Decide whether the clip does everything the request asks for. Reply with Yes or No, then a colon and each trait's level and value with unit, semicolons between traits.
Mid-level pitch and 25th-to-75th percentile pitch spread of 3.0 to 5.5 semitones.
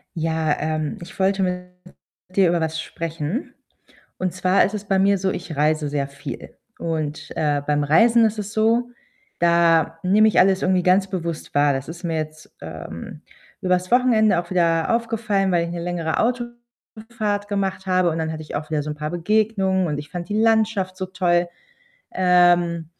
Yes: medium, 180 Hz; average, 3.9 semitones